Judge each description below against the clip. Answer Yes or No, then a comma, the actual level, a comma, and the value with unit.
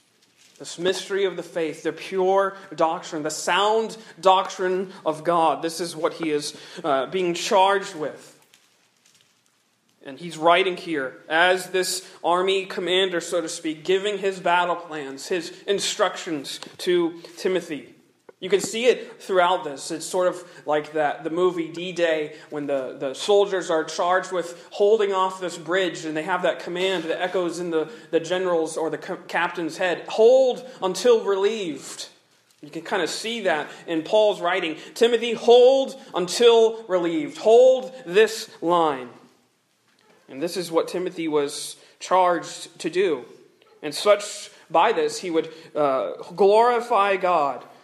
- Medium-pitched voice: Yes, medium, 180 Hz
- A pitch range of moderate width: Yes, average, 3.8 semitones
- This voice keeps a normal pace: Yes, average, 150 wpm